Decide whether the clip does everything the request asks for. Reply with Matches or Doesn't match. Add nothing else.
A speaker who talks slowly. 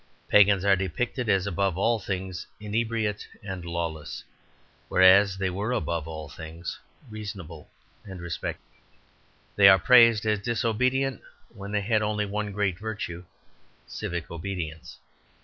Matches